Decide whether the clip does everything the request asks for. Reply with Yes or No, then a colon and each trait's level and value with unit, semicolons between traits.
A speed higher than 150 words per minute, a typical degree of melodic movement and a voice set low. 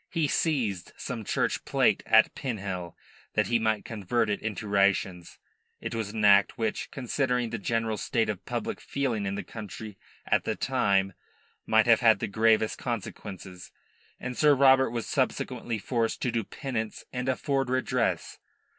Yes: average, 160 wpm; average, 3.7 semitones; low, 110 Hz